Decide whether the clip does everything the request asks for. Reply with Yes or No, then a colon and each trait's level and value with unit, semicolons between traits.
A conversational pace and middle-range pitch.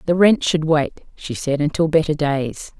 Yes: average, 195 wpm; medium, 155 Hz